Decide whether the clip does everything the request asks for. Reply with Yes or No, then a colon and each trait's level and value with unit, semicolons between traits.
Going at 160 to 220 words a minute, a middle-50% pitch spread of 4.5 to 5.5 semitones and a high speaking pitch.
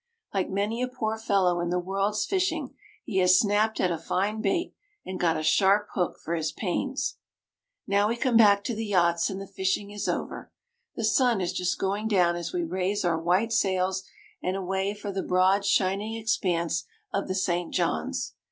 No: average, 190 wpm; average, 2.8 semitones; high, 195 Hz